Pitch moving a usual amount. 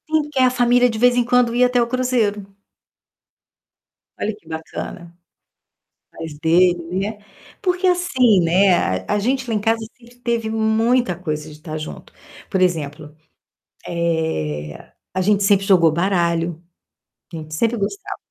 No: wide, 6.6 semitones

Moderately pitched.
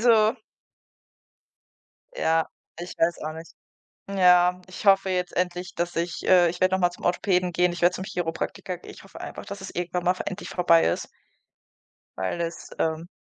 Yes: medium, 180 Hz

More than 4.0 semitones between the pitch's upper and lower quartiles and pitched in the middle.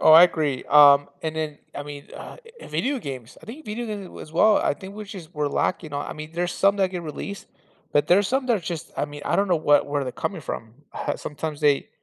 Yes: average, 5.2 semitones; medium, 160 Hz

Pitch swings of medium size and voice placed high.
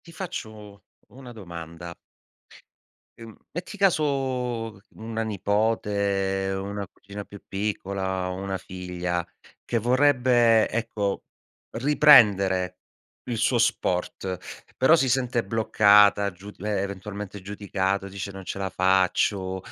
No: average, 3.4 semitones; low, 100 Hz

